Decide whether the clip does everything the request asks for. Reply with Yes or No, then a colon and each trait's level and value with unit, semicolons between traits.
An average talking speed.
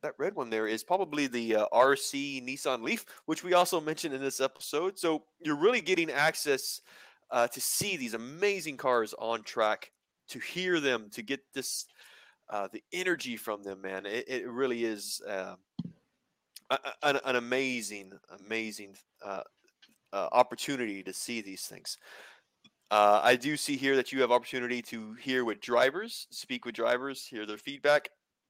Yes: average, 165 wpm